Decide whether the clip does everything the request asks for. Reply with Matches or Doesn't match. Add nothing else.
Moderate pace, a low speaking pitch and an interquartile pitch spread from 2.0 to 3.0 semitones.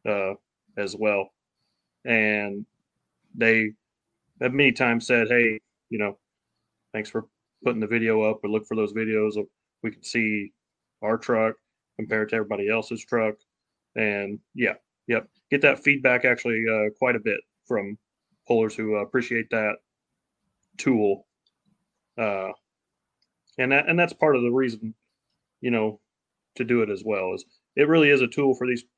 Matches